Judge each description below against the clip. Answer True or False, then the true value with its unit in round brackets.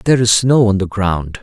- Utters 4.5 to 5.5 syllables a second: True (5.1 syllables/s)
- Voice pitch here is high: False (105 Hz)